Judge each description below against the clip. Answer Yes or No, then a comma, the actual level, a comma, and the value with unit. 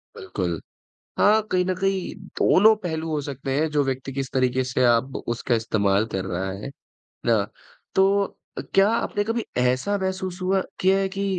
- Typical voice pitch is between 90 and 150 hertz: Yes, medium, 140 Hz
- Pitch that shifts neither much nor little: No, wide, 8.3 semitones